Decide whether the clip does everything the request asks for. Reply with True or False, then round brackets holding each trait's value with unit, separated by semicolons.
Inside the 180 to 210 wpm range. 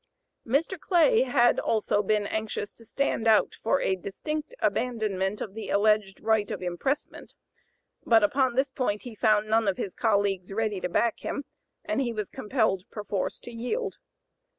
False (165 wpm)